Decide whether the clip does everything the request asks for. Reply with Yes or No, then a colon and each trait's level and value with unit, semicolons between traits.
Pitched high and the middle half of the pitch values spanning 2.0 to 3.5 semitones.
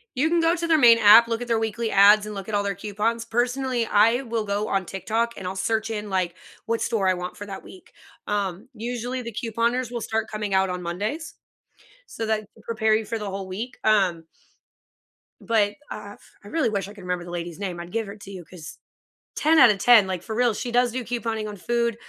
Yes: high, 215 Hz; average, 3.0 semitones